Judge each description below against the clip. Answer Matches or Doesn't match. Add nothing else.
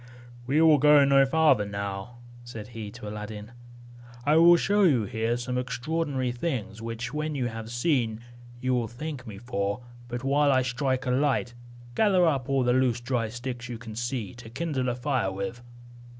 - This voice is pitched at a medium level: Doesn't match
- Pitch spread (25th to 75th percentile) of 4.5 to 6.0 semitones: Doesn't match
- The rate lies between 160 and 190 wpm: Matches